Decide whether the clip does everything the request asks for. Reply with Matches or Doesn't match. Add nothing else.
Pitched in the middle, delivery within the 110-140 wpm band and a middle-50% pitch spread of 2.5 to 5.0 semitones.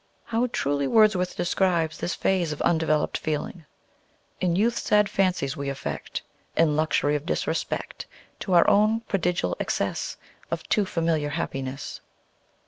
Matches